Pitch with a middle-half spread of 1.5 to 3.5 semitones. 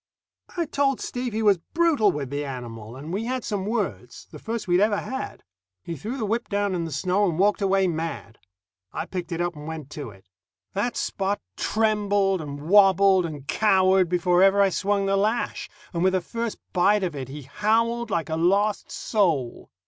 No: average, 4.3 semitones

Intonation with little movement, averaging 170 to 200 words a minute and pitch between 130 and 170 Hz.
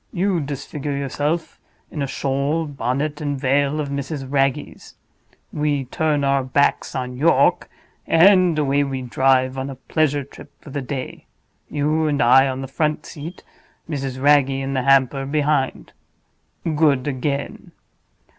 No: narrow, 2.0 semitones; average, 140 wpm; medium, 140 Hz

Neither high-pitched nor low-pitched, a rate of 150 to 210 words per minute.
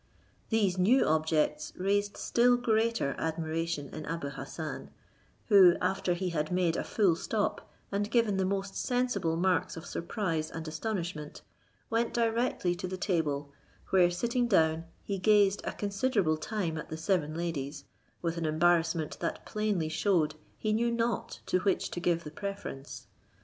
Yes: medium, 180 Hz; average, 155 wpm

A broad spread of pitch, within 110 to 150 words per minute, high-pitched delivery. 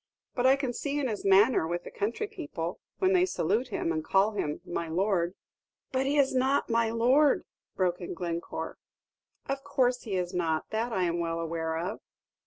No: wide, 7.2 semitones; average, 195 wpm; high, 210 Hz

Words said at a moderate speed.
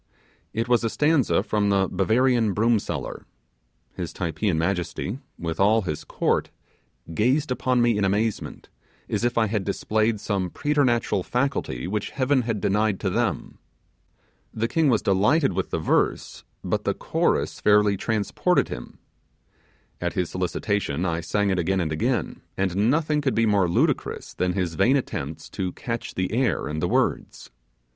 Yes: average, 160 wpm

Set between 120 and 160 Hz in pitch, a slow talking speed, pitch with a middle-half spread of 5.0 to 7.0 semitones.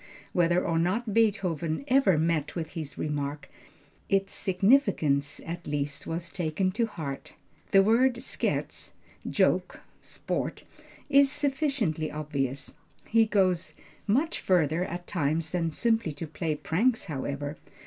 No: medium, 170 Hz; slow, 125 wpm; wide, 5.6 semitones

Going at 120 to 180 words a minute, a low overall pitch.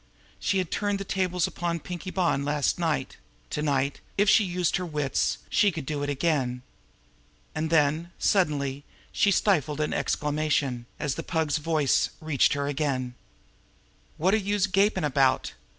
No: average, 155 wpm; medium, 155 Hz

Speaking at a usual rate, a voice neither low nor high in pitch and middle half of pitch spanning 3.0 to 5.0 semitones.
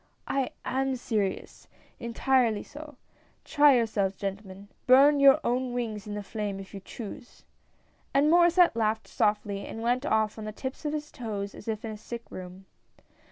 No: average, 175 wpm; high, 230 Hz; average, 4.5 semitones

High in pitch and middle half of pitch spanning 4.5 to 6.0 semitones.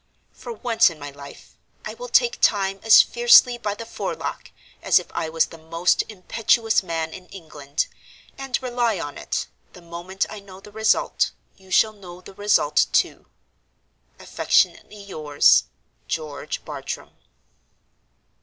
Yes: high, 195 Hz; average, 5.2 semitones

